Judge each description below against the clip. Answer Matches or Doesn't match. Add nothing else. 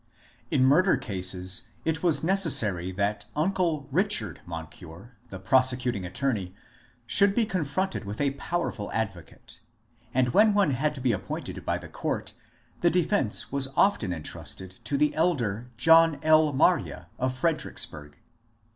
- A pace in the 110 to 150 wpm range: Matches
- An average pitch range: Doesn't match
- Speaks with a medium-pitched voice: Doesn't match